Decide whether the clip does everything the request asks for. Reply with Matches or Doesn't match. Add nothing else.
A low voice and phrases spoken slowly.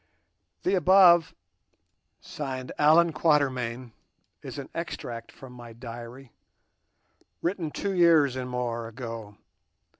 Matches